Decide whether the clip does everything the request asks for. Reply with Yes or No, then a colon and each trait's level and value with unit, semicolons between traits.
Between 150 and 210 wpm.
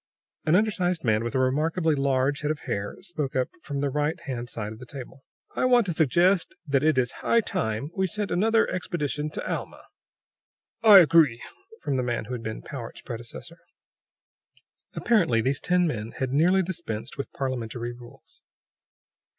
Yes: average, 165 wpm